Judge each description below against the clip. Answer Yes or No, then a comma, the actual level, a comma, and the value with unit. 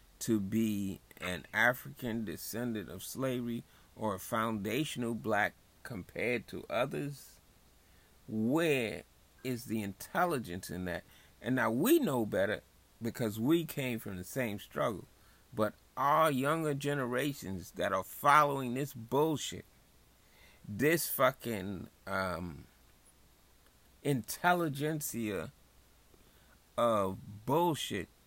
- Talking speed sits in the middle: No, slow, 100 wpm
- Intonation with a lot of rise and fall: Yes, wide, 5.7 semitones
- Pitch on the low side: Yes, low, 115 Hz